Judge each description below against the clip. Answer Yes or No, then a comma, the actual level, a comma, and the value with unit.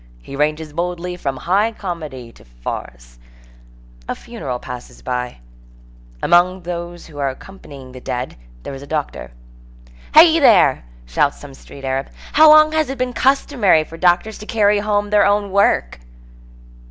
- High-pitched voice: No, medium, 175 Hz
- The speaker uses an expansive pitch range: Yes, wide, 7.5 semitones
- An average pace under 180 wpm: Yes, average, 150 wpm